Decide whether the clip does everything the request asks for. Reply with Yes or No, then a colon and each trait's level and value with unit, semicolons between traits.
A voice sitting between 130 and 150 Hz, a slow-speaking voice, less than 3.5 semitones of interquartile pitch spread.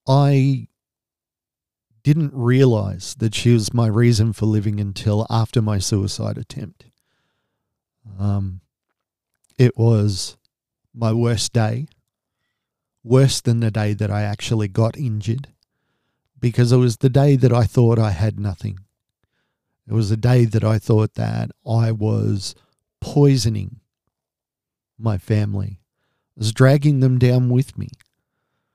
No: low, 115 Hz; slow, 125 wpm; average, 2.8 semitones